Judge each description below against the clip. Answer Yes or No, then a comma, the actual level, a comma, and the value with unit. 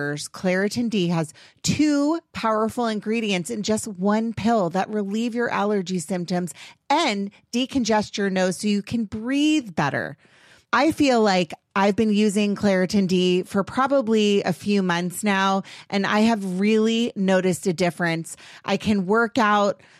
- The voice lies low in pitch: No, high, 205 Hz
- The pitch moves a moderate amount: Yes, average, 3.3 semitones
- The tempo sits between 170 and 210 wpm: No, average, 145 wpm